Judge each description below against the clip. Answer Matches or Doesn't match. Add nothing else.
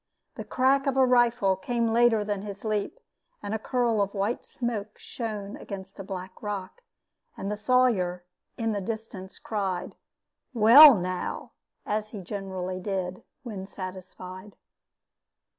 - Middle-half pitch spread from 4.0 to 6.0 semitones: Doesn't match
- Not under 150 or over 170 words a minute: Doesn't match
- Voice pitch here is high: Matches